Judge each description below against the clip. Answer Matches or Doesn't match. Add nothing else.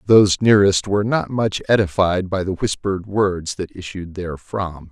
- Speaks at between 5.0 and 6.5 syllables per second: Matches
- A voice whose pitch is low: Matches